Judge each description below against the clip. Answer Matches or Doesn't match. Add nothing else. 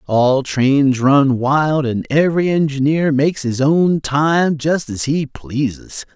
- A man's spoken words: Matches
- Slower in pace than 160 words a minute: Matches